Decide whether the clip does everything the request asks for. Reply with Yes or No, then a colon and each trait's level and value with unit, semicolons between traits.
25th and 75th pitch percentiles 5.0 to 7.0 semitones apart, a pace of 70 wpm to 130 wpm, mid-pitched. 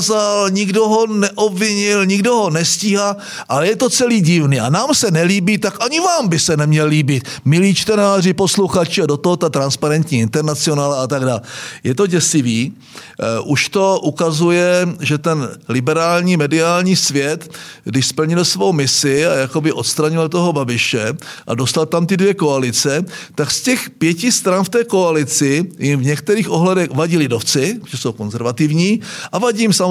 No: wide, 5.4 semitones; average, 160 wpm; medium, 165 Hz